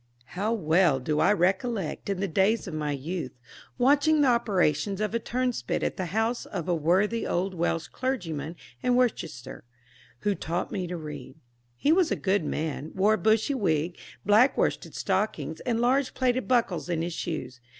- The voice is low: No, high, 190 Hz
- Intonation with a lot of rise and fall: Yes, wide, 6.4 semitones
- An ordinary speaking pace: Yes, average, 175 wpm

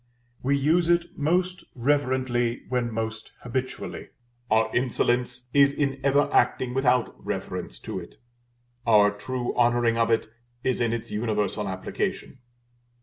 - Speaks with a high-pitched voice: No, low, 125 Hz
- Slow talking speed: Yes, slow, 130 wpm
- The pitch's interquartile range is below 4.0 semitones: Yes, average, 3.0 semitones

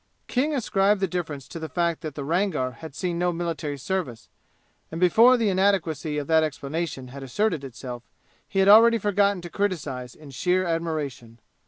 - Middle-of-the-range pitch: Yes, medium, 165 Hz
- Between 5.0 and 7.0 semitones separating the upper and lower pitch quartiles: Yes, average, 5.3 semitones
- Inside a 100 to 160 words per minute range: No, average, 175 wpm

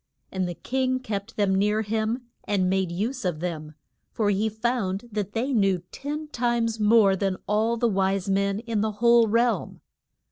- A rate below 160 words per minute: No, average, 175 wpm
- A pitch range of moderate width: Yes, average, 3.4 semitones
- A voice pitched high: Yes, high, 210 Hz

